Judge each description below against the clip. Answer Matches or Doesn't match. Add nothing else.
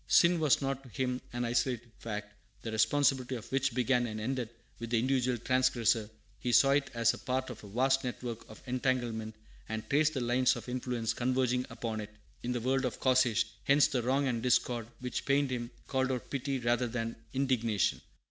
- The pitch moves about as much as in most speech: Doesn't match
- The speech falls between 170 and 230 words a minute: Matches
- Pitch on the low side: Matches